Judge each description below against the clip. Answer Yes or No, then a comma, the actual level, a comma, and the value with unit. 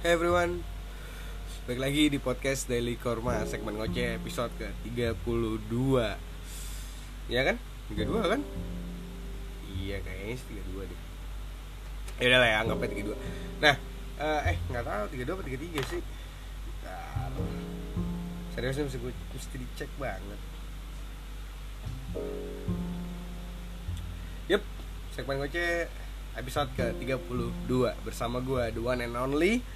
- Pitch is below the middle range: Yes, very low, 95 Hz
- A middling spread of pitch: No, wide, 6.5 semitones